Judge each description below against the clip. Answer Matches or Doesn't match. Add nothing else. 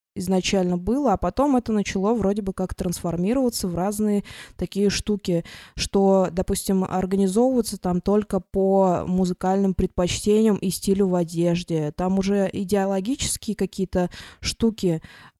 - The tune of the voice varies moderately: Doesn't match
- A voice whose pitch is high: Matches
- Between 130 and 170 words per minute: Doesn't match